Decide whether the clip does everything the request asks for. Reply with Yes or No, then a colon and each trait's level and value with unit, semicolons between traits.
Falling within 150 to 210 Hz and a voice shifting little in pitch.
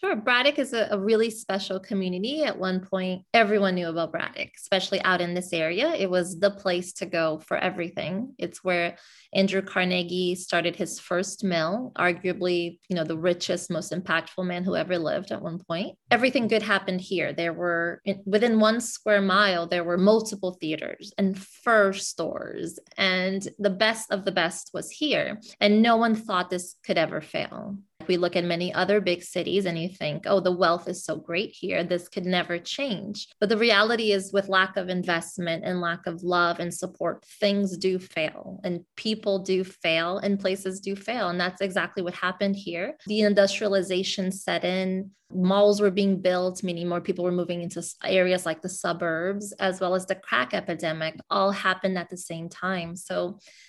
Yes: medium, 185 Hz; narrow, 2.3 semitones